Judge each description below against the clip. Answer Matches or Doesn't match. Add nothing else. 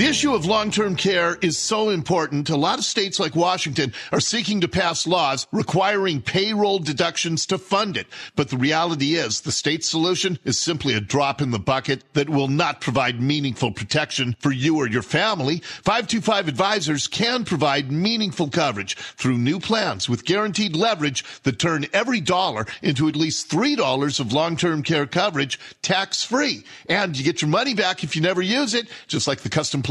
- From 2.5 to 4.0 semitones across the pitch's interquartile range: Doesn't match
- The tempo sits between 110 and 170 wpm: Doesn't match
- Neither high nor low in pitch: Matches